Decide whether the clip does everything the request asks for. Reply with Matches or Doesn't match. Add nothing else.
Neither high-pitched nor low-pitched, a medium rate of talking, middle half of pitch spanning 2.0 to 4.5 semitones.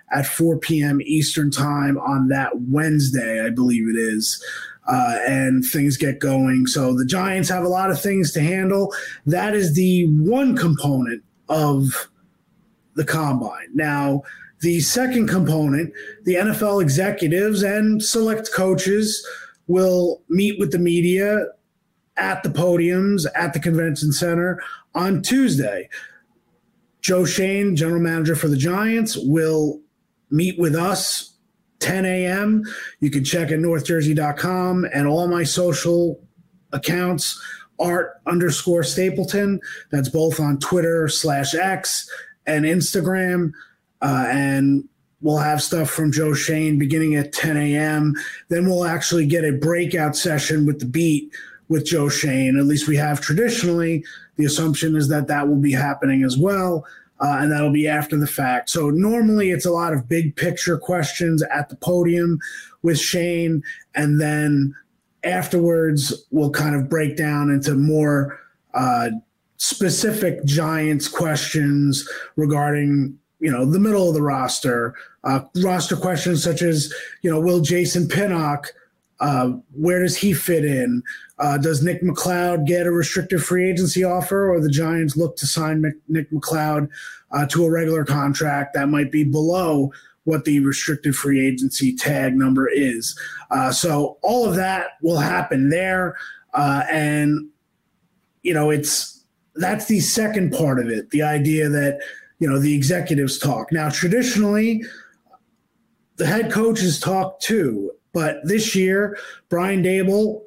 Matches